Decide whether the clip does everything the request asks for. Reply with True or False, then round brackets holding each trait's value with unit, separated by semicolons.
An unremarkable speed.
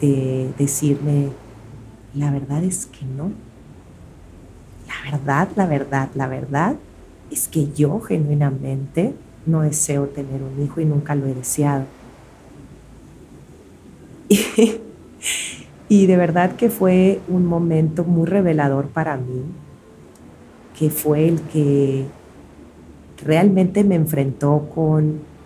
False (110 wpm)